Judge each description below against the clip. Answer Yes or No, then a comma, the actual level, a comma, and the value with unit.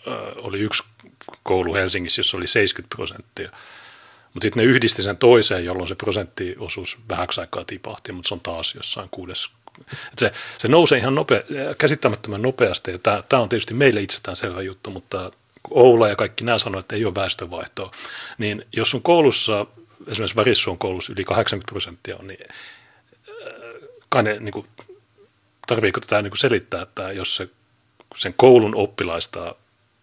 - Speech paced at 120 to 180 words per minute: Yes, fast, 155 wpm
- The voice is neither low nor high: Yes, medium, 155 Hz